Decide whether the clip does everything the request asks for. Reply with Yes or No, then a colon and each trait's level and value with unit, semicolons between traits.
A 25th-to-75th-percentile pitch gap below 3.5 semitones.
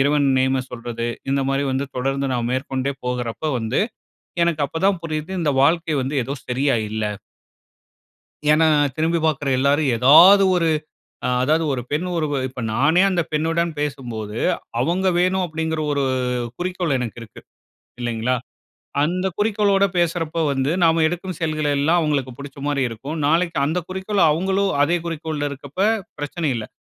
No: average, 4.0 semitones